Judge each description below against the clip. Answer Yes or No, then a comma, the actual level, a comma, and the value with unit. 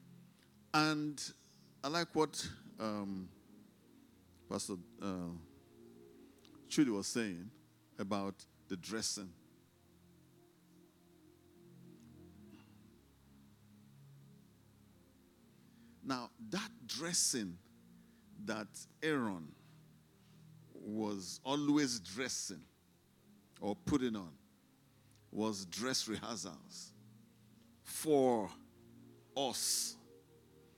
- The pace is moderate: No, slow, 55 wpm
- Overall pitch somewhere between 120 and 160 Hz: No, low, 100 Hz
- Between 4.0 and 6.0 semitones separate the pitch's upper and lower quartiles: Yes, average, 5.1 semitones